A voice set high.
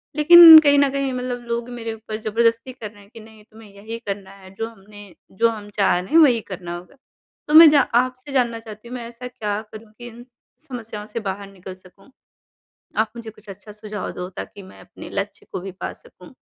Yes: high, 225 Hz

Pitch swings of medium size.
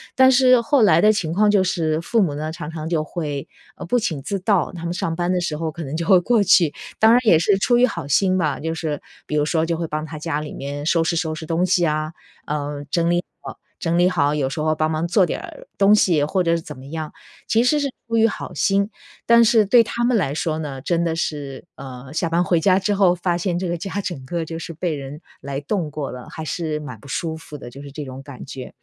Yes: average, 4.0 semitones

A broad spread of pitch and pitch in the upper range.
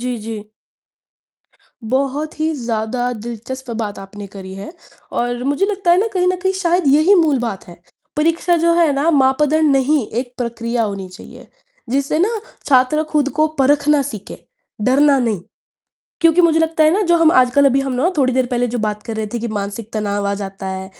Yes: wide, 5.9 semitones; very high, 260 Hz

